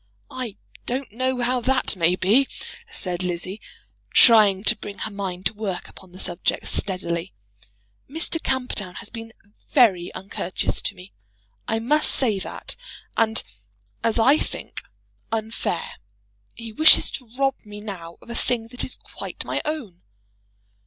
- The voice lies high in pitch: Yes, high, 220 Hz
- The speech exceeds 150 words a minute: No, average, 145 wpm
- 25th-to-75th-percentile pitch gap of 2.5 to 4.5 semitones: No, average, 5.1 semitones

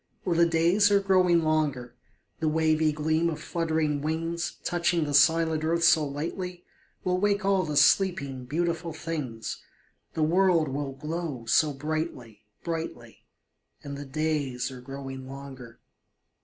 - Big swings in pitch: No, average, 3.4 semitones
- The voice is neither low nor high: Yes, medium, 155 Hz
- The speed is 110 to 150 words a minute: Yes, average, 140 wpm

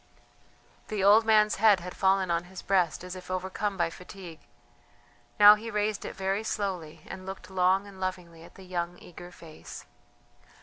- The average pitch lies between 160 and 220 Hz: Yes, high, 190 Hz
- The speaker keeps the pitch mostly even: Yes, narrow, 2.2 semitones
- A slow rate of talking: No, average, 170 wpm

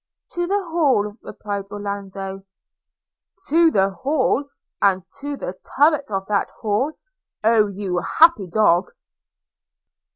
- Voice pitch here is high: Yes, high, 210 Hz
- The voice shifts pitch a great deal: Yes, wide, 6.8 semitones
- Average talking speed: No, slow, 125 wpm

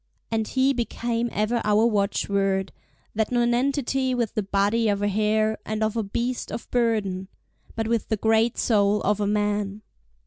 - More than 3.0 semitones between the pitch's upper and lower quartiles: No, narrow, 2.4 semitones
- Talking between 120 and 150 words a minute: No, average, 160 wpm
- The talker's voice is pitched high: Yes, high, 220 Hz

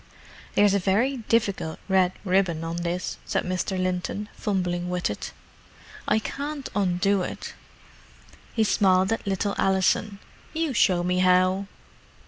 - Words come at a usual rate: No, slow, 130 wpm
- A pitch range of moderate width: No, narrow, 2.3 semitones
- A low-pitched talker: No, high, 190 Hz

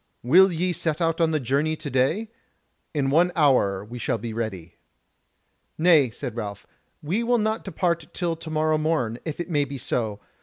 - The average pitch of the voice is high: No, medium, 155 Hz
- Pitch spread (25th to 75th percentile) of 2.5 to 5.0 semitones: No, wide, 5.6 semitones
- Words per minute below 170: No, average, 180 wpm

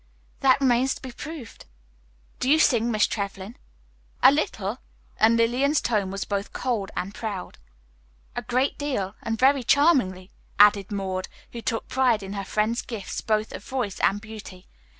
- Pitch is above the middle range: Yes, high, 225 Hz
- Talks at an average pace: Yes, average, 160 wpm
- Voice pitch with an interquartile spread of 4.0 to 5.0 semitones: Yes, average, 4.3 semitones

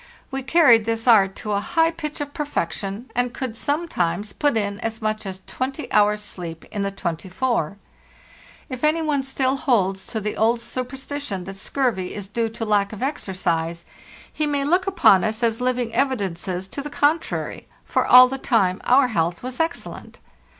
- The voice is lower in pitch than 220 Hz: No, high, 230 Hz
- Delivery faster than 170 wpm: Yes, average, 180 wpm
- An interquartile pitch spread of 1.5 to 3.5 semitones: No, wide, 5.5 semitones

